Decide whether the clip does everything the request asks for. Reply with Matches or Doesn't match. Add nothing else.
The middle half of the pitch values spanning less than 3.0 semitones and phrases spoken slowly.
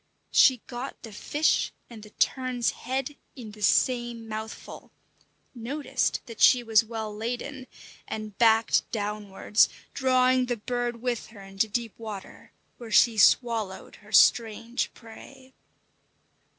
Matches